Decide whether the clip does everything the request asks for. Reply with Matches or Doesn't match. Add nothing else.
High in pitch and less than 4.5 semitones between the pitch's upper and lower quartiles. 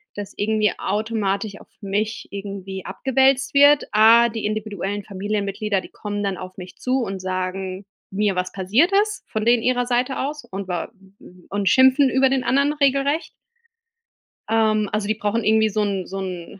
Matches